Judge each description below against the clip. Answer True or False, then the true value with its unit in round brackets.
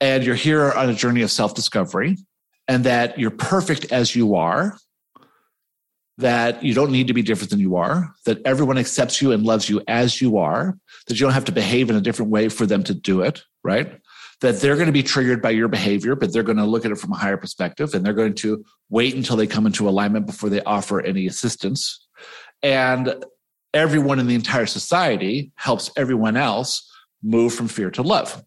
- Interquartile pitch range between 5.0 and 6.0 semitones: False (3.8 semitones)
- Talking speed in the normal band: False (215 wpm)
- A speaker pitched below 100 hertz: False (120 Hz)